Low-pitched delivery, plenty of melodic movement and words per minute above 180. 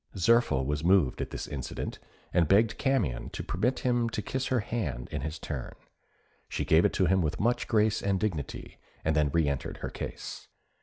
Yes: very low, 90 Hz; wide, 7.2 semitones; average, 190 wpm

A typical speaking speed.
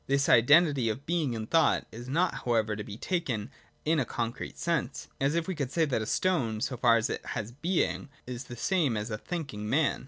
No: fast, 220 wpm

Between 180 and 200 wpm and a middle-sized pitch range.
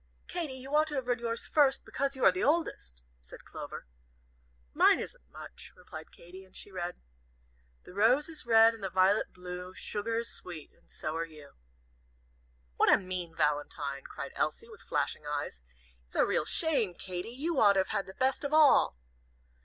No: average, 185 wpm; wide, 7.3 semitones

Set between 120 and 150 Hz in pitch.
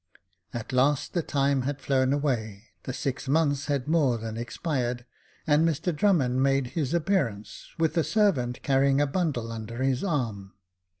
Yes: low, 135 Hz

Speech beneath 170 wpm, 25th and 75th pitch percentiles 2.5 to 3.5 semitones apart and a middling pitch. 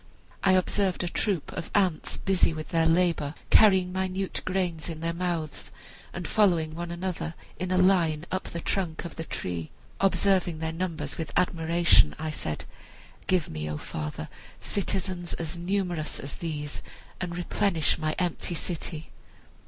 Yes: average, 150 wpm; average, 2.8 semitones; medium, 170 Hz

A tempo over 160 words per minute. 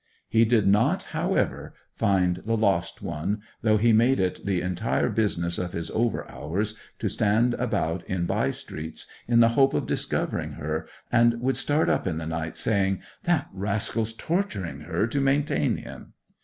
Yes: average, 170 wpm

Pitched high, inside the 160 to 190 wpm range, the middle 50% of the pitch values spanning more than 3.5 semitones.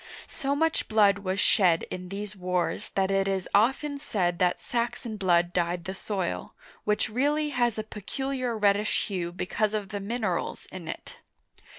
Yes: high, 205 Hz; average, 165 wpm; average, 4.2 semitones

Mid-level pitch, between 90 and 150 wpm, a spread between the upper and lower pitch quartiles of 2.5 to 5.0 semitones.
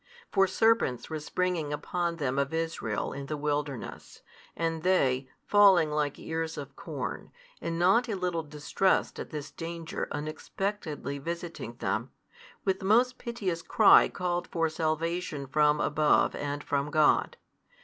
Yes: medium, 160 Hz; average, 140 wpm; average, 3.6 semitones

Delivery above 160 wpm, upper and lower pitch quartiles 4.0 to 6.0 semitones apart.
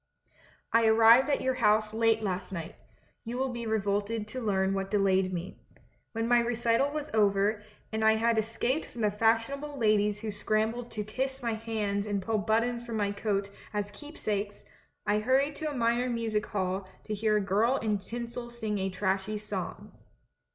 No: average, 180 wpm; narrow, 2.5 semitones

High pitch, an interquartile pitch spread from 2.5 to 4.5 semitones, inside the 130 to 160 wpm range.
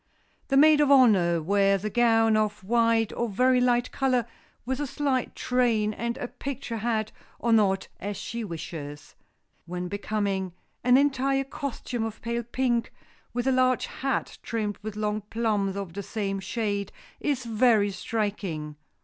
Yes: high, 225 Hz; average, 3.7 semitones; average, 155 wpm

